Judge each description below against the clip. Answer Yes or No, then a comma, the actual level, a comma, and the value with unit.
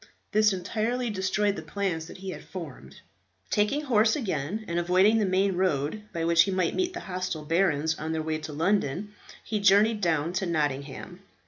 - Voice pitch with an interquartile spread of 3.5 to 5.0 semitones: Yes, average, 4.5 semitones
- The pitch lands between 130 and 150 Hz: No, medium, 185 Hz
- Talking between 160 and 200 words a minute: Yes, average, 185 wpm